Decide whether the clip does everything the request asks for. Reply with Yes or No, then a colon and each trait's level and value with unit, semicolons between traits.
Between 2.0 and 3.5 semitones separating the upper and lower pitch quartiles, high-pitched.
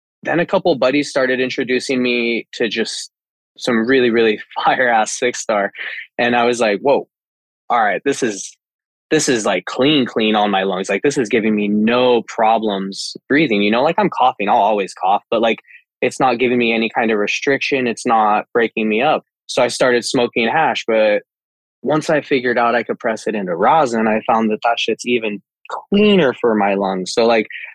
No: average, 2.9 semitones; low, 115 Hz